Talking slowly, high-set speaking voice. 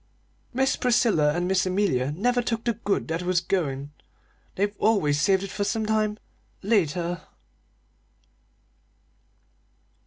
Yes: slow, 115 wpm; high, 195 Hz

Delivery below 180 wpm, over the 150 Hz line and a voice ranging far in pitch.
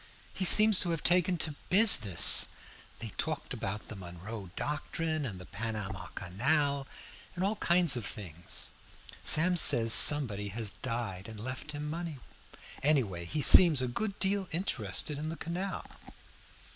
No: average, 145 wpm; medium, 140 Hz; wide, 8.2 semitones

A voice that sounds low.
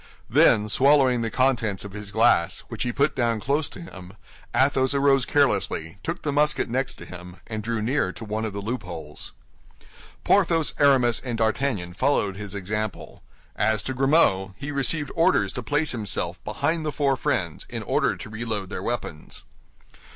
Yes: low, 115 Hz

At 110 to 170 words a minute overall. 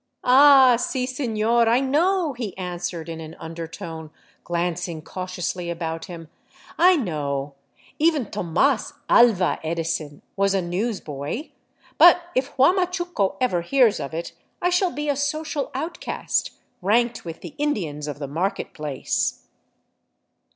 Yes: slow, 135 wpm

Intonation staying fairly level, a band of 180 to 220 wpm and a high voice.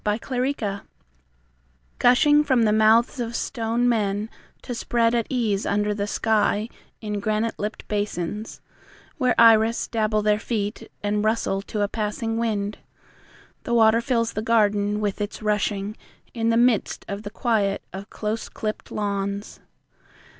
No: narrow, 1.9 semitones; average, 145 wpm; high, 215 Hz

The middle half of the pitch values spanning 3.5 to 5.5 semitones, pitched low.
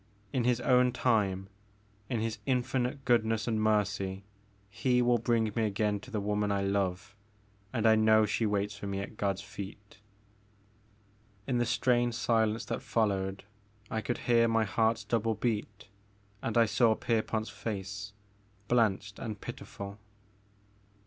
No: narrow, 2.6 semitones; low, 110 Hz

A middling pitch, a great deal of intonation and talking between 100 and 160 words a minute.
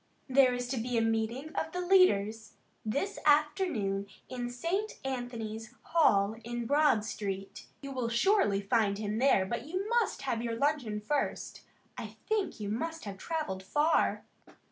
No: high, 245 Hz; wide, 5.9 semitones; average, 155 wpm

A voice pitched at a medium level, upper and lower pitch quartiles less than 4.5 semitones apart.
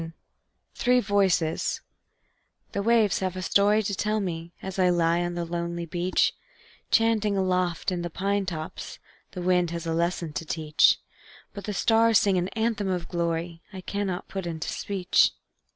Yes: medium, 180 Hz; average, 2.9 semitones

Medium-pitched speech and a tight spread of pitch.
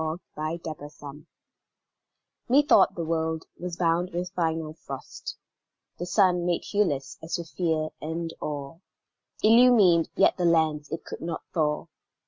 Yes: medium, 165 Hz; narrow, 2.2 semitones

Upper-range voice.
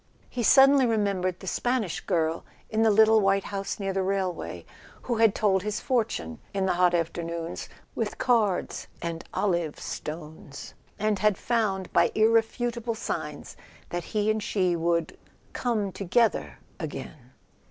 Yes: high, 195 Hz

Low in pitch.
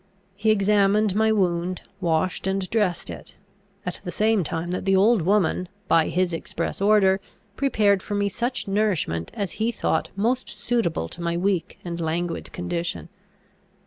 No: high, 190 Hz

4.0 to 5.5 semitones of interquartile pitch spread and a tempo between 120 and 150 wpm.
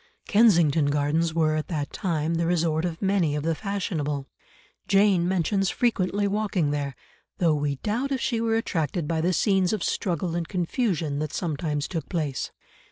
No: average, 4.3 semitones; average, 165 wpm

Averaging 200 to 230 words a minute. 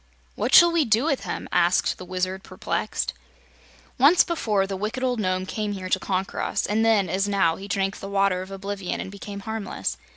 Yes: fast, 205 wpm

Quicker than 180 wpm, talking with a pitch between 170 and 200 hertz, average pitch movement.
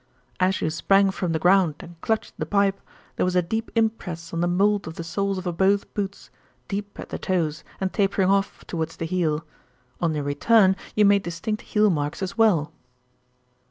Yes: average, 195 wpm; medium, 185 Hz; average, 3.1 semitones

